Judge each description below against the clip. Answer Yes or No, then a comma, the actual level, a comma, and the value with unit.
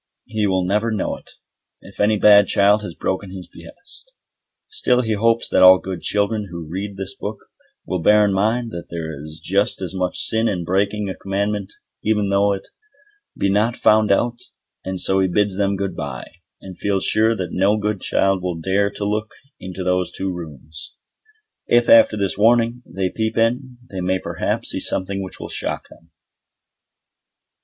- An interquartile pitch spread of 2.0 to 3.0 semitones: Yes, narrow, 2.5 semitones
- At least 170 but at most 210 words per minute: Yes, average, 180 wpm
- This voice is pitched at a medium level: No, low, 100 Hz